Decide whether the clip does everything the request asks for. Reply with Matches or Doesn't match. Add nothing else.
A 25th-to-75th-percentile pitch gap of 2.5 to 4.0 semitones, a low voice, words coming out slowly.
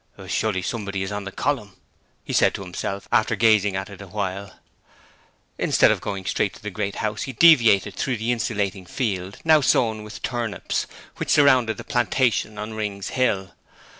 Doesn't match